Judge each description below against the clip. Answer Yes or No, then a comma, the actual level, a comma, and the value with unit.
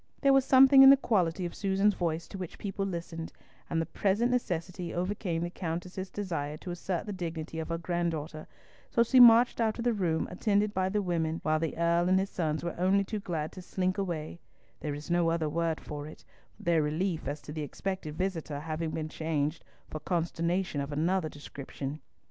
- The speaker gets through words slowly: No, average, 195 wpm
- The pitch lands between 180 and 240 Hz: No, medium, 170 Hz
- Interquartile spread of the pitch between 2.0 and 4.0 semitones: Yes, average, 3.4 semitones